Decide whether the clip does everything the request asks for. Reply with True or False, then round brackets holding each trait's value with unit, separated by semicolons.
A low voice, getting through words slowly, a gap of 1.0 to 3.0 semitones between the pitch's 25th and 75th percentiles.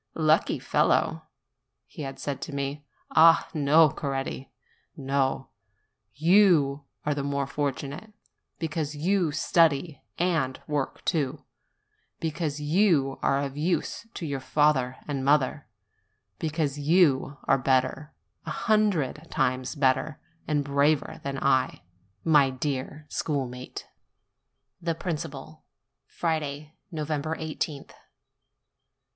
False (145 Hz; 105 wpm; 2.5 semitones)